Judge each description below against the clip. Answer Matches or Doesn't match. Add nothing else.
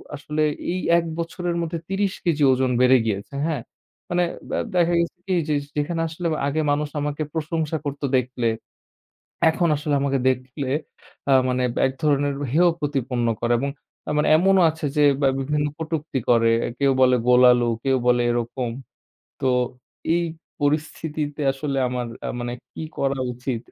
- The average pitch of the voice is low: Doesn't match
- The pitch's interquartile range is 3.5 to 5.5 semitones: Matches